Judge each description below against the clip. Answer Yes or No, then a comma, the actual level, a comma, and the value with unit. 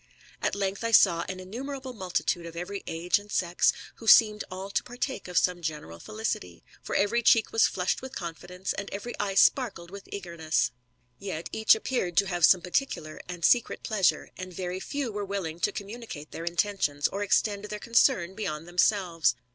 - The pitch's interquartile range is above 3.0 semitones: Yes, average, 3.8 semitones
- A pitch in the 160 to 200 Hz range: Yes, high, 190 Hz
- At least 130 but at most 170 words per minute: No, average, 185 wpm